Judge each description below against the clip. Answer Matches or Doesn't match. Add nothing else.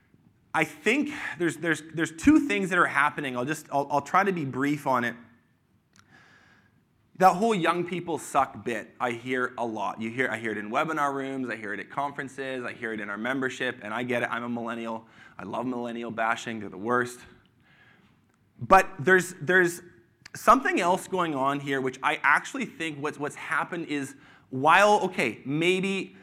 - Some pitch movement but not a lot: Doesn't match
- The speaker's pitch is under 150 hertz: Matches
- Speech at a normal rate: Matches